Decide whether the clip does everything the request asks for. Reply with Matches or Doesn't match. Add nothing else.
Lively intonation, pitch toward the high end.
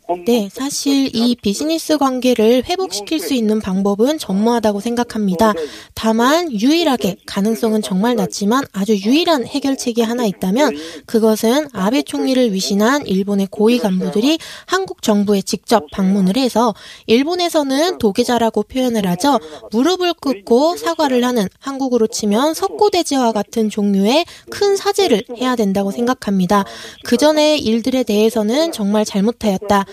Doesn't match